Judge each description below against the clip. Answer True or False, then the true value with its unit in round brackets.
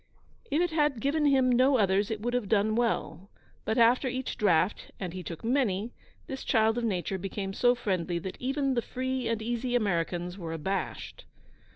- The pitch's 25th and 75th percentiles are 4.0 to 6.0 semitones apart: True (4.8 semitones)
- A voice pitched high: True (225 Hz)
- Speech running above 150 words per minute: True (185 wpm)